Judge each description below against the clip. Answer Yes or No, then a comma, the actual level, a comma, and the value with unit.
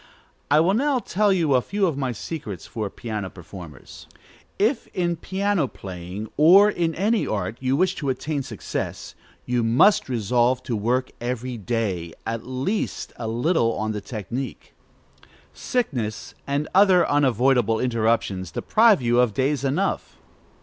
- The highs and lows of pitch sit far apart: Yes, wide, 7.3 semitones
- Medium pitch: No, low, 130 Hz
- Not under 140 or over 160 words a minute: Yes, average, 145 wpm